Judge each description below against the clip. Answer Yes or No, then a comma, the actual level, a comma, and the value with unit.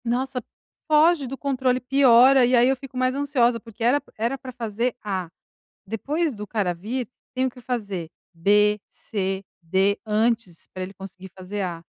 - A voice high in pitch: Yes, high, 235 Hz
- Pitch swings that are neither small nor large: Yes, average, 4.6 semitones